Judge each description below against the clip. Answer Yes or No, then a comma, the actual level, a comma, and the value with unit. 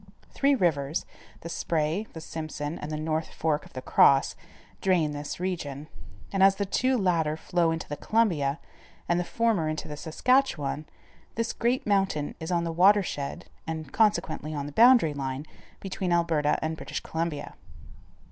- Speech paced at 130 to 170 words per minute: Yes, average, 160 wpm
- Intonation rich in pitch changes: No, average, 4.3 semitones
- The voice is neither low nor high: Yes, medium, 165 Hz